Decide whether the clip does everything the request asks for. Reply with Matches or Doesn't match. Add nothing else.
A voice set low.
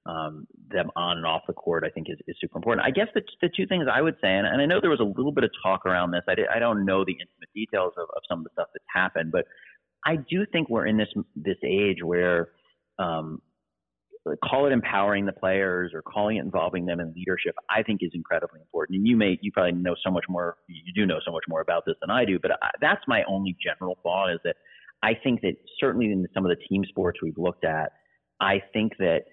Matches